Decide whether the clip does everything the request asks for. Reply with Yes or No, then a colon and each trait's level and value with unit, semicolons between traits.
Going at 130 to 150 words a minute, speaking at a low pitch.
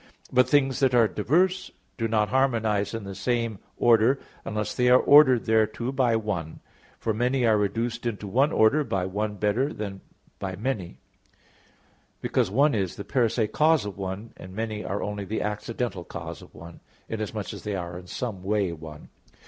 No: average, 180 wpm; low, 110 Hz